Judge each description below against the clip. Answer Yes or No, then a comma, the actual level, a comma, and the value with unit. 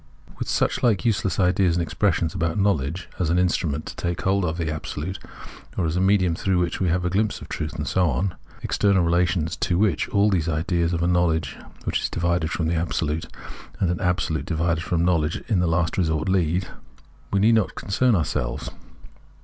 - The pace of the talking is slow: No, average, 200 wpm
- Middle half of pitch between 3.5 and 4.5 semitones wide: No, narrow, 2.6 semitones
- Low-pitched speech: Yes, very low, 85 Hz